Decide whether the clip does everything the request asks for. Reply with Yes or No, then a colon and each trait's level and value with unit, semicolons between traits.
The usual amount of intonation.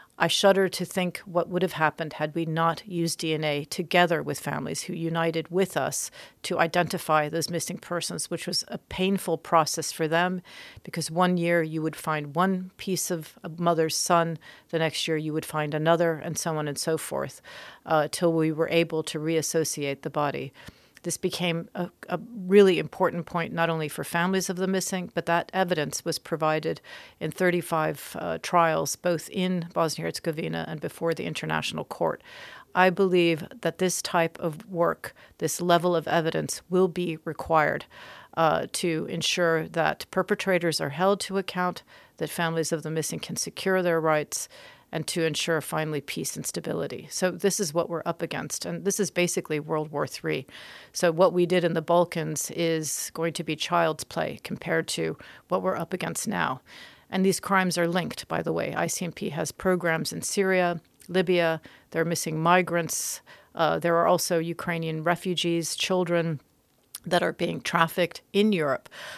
No: narrow, 2.0 semitones